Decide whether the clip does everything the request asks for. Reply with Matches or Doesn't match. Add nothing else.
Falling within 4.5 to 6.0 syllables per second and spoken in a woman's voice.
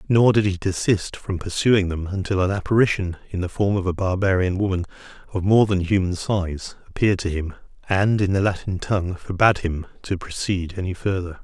Doesn't match